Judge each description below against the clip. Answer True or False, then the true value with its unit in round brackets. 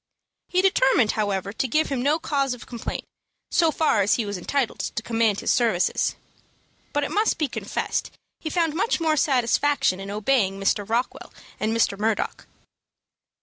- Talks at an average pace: True (165 wpm)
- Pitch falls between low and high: False (245 Hz)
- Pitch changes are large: True (5.9 semitones)